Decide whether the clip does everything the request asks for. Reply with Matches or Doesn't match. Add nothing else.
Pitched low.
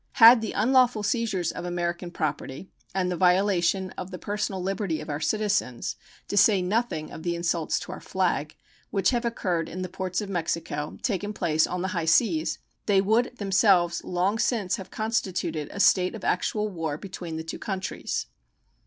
Doesn't match